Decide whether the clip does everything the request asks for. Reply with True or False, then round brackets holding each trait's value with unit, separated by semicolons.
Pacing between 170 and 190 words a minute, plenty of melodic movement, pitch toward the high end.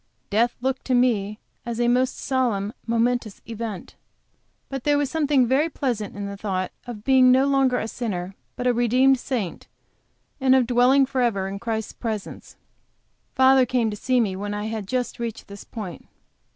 False (175 wpm; 3.6 semitones; 240 Hz)